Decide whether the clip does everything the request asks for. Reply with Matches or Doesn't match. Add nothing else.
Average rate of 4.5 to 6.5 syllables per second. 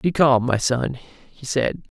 Doesn't match